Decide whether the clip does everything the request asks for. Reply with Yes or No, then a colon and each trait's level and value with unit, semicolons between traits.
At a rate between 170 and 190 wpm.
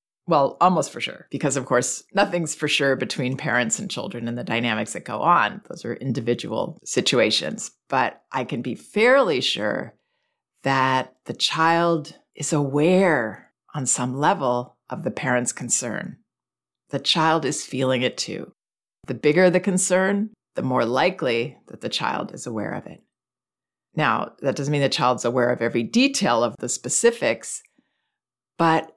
No: average, 155 wpm